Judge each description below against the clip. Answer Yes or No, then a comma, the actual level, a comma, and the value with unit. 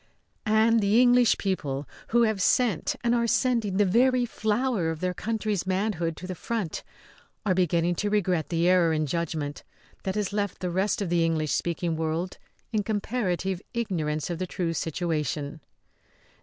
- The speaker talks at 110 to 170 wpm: Yes, average, 165 wpm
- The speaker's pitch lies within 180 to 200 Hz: Yes, medium, 185 Hz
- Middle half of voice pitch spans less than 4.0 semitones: No, average, 4.6 semitones